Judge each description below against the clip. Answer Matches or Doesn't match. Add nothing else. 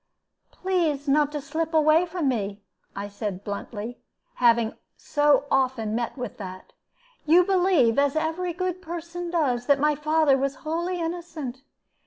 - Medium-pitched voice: Doesn't match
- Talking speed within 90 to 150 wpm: Matches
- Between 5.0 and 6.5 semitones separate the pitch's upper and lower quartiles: Matches